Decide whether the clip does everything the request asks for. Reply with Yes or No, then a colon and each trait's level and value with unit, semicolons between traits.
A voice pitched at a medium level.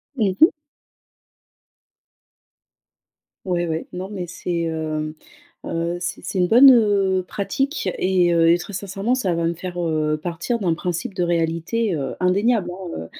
Yes: medium, 180 Hz